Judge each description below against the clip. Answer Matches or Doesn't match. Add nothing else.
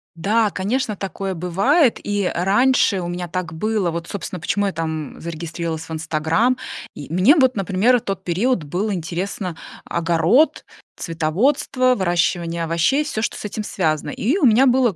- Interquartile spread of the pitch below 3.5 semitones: Doesn't match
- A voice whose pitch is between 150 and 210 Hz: Matches